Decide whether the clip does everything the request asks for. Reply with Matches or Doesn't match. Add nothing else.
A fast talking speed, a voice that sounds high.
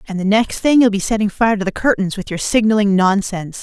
Matches